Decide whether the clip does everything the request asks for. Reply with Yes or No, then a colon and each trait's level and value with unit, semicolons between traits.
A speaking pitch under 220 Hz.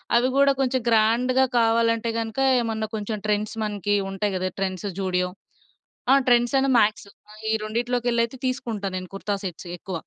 No: high, 225 Hz